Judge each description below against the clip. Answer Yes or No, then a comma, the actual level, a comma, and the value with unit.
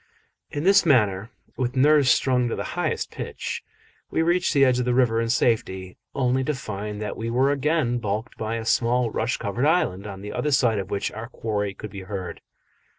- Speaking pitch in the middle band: No, low, 120 Hz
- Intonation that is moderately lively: Yes, average, 4.1 semitones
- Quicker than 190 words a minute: Yes, fast, 205 wpm